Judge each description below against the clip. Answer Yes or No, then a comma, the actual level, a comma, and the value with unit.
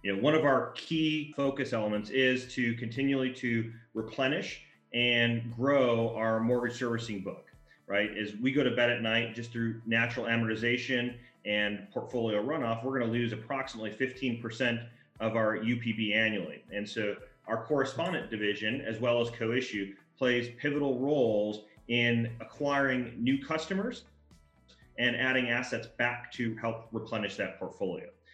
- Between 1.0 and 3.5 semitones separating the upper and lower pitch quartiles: Yes, narrow, 2.6 semitones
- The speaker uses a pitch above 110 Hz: Yes, low, 120 Hz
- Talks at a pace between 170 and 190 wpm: No, average, 145 wpm